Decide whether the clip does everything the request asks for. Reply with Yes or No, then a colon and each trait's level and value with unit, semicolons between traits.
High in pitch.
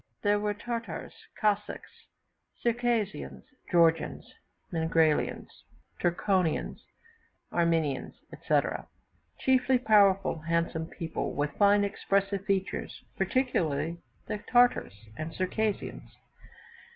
Yes: high, 195 Hz